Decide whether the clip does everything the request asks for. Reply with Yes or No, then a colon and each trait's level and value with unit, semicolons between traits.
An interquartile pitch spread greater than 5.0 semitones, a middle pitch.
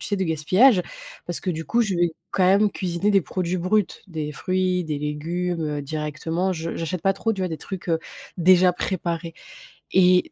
No: narrow, 2.5 semitones; medium, 180 Hz